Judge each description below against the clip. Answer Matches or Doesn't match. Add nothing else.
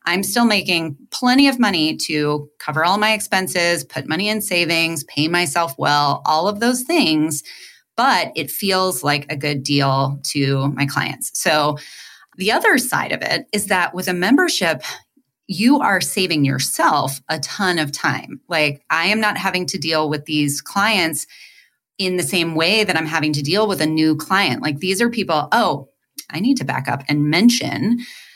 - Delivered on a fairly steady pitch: Doesn't match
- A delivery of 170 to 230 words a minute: Matches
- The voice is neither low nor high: Matches